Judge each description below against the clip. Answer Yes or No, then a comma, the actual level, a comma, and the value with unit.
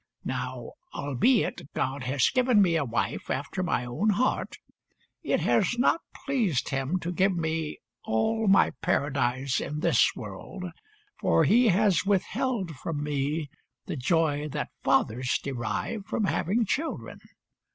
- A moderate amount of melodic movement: No, wide, 7.1 semitones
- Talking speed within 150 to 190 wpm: No, slow, 135 wpm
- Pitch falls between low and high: Yes, medium, 165 Hz